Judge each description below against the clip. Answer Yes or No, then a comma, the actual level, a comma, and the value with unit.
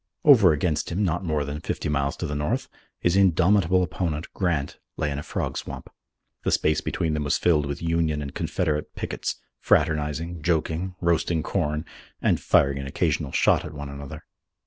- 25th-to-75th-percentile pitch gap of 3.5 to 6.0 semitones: No, average, 2.8 semitones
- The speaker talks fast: No, average, 175 wpm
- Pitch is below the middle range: Yes, very low, 80 Hz